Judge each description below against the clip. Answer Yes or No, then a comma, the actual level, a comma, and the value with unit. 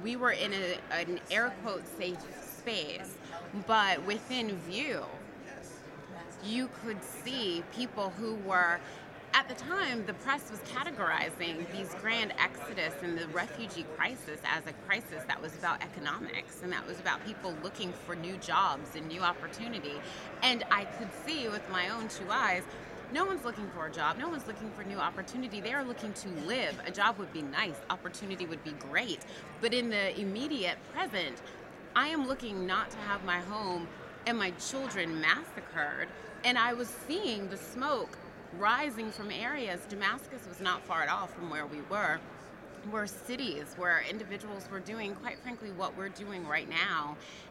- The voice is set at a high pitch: Yes, high, 205 Hz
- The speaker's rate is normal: Yes, average, 170 wpm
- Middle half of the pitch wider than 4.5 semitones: Yes, average, 4.9 semitones